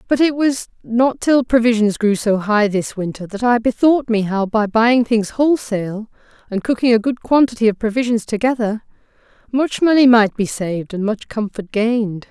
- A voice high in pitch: Yes, high, 225 Hz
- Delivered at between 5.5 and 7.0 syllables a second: No, 5.0 syllables/s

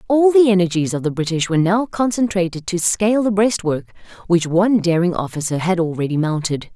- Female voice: Yes, female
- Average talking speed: Yes, average, 180 wpm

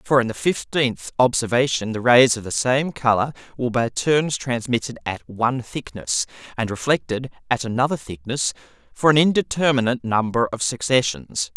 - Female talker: No, male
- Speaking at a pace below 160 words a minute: Yes, average, 150 wpm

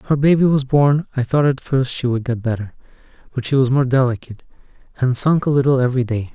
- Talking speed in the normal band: No, fast, 225 wpm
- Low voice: Yes, low, 130 Hz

